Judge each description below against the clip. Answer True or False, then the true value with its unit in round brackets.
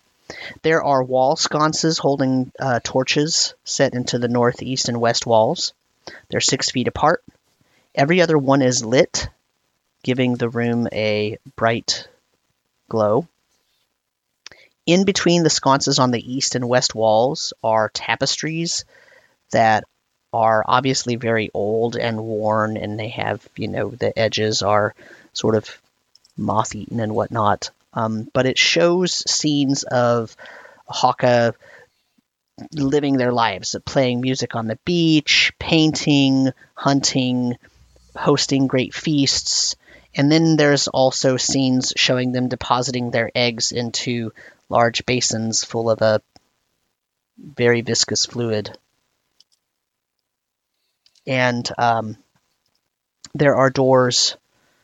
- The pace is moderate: False (115 wpm)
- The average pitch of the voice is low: True (125 Hz)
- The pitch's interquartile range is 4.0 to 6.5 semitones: False (3.2 semitones)